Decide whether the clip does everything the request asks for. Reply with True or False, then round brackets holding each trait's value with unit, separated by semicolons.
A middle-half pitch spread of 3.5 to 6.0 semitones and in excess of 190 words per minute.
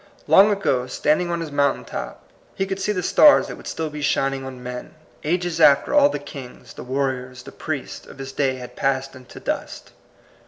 True (4.9 semitones; 205 wpm)